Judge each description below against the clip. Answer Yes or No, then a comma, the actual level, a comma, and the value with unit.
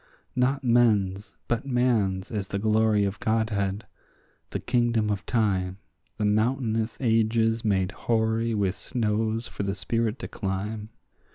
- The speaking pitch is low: Yes, low, 110 Hz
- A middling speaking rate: No, slow, 130 wpm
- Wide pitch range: No, narrow, 2.4 semitones